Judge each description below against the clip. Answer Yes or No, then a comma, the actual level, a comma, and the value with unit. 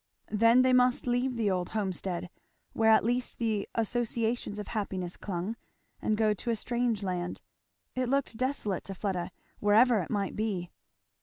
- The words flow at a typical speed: Yes, average, 160 wpm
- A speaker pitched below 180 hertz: No, high, 220 Hz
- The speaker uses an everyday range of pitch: Yes, average, 3.7 semitones